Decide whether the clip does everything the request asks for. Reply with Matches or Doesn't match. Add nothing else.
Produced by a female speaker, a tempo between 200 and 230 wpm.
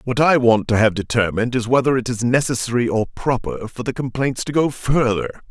Doesn't match